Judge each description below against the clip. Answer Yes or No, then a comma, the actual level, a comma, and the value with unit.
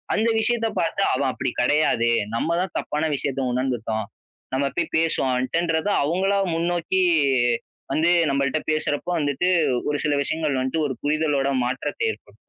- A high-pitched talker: No, medium, 150 Hz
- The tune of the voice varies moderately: Yes, average, 4.0 semitones